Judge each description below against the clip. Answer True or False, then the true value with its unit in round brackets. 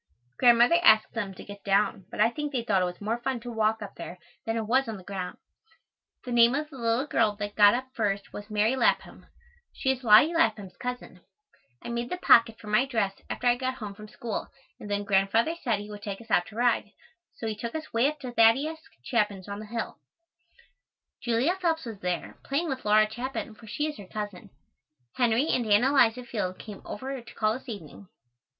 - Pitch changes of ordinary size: True (3.4 semitones)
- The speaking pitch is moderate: False (225 Hz)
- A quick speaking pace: True (215 wpm)